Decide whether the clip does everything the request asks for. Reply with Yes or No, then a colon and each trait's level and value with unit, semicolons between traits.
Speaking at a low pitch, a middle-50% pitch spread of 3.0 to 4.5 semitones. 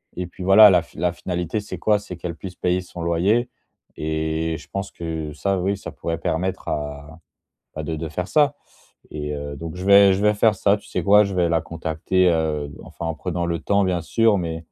Yes: very low, 85 Hz; average, 3.4 semitones